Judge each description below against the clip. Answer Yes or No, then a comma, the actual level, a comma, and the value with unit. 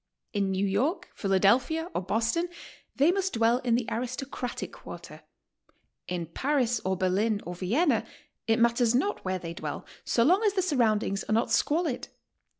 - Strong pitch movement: Yes, wide, 6.6 semitones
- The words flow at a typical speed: Yes, average, 155 wpm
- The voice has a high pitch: Yes, high, 235 Hz